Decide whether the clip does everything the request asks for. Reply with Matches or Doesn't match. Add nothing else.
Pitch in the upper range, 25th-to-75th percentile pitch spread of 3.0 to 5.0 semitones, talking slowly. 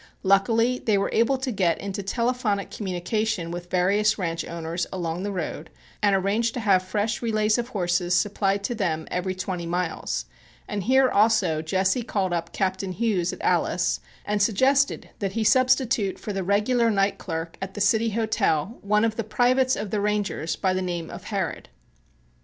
Doesn't match